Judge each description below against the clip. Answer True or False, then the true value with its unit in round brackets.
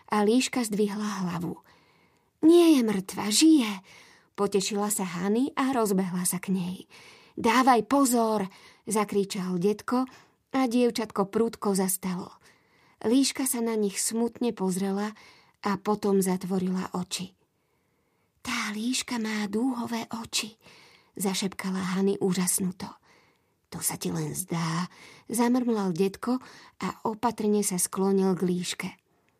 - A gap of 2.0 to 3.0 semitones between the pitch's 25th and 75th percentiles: False (3.5 semitones)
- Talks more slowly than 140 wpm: True (110 wpm)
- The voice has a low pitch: False (205 Hz)